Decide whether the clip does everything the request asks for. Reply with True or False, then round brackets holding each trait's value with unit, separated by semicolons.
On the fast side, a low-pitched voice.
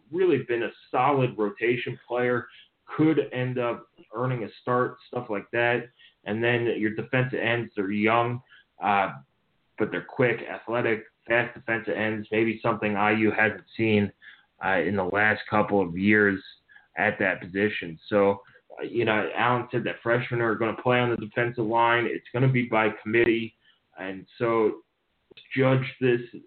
False (160 wpm; 115 Hz)